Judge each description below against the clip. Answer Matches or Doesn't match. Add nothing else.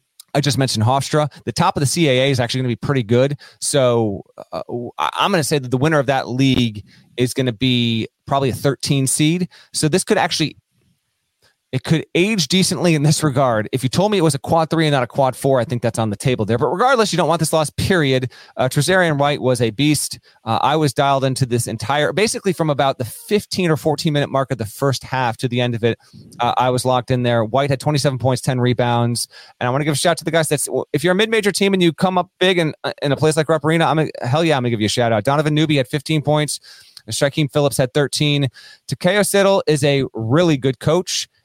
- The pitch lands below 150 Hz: Matches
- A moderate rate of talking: Doesn't match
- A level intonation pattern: Doesn't match